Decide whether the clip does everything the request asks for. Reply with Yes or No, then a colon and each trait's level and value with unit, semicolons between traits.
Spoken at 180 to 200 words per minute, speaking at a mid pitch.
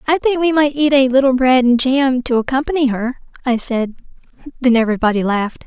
No: average, 190 wpm; very high, 260 Hz